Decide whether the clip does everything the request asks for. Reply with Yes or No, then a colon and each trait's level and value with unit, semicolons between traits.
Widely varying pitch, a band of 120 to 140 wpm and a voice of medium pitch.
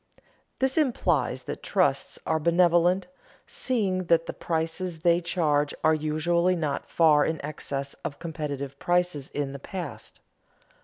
No: average, 3.1 semitones; slow, 135 wpm; medium, 165 Hz